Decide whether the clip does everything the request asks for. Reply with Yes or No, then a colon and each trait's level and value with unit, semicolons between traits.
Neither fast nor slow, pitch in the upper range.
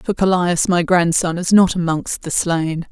No: average, 185 wpm; medium, 175 Hz